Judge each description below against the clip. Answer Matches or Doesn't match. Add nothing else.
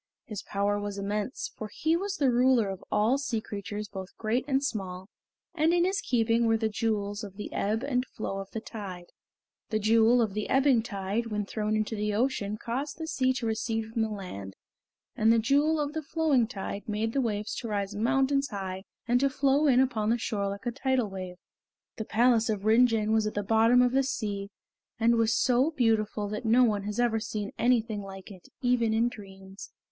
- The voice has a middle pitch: Doesn't match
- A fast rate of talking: Matches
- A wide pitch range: Doesn't match